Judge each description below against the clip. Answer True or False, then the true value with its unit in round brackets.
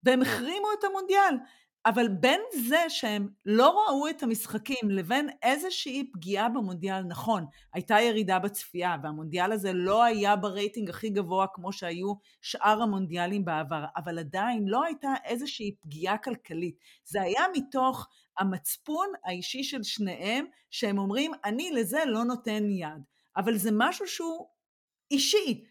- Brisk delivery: False (135 wpm)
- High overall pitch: True (220 Hz)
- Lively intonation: True (5.9 semitones)